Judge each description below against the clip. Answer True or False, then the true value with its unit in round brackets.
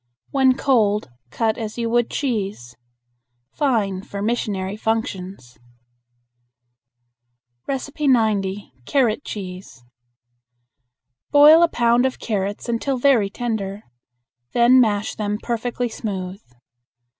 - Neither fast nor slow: False (95 wpm)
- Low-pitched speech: False (220 Hz)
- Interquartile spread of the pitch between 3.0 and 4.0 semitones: True (3.5 semitones)